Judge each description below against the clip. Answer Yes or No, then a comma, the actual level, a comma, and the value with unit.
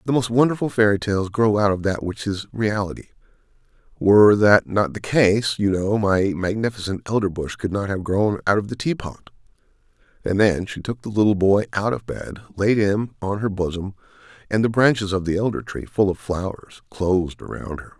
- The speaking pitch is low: Yes, low, 105 Hz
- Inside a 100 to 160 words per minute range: No, average, 195 wpm